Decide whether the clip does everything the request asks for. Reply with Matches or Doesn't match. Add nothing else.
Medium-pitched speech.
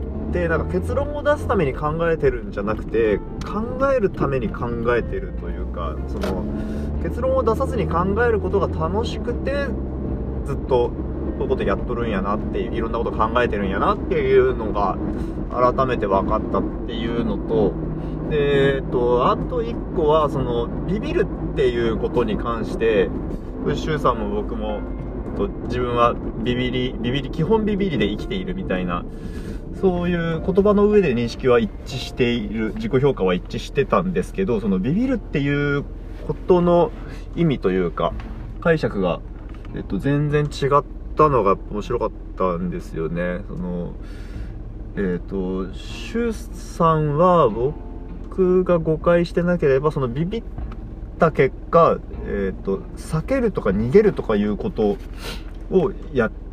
Doesn't match